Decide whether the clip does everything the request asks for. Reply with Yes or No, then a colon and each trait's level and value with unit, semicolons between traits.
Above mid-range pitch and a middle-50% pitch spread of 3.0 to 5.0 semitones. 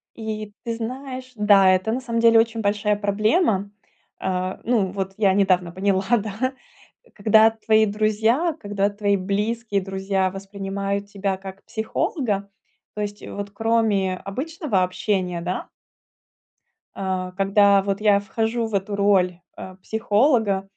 No: high, 205 Hz; narrow, 2.4 semitones